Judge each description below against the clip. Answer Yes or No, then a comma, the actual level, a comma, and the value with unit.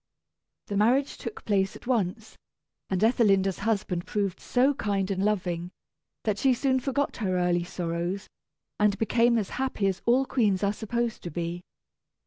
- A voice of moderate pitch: No, high, 205 Hz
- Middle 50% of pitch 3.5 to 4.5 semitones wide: Yes, average, 4.2 semitones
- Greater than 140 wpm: Yes, average, 155 wpm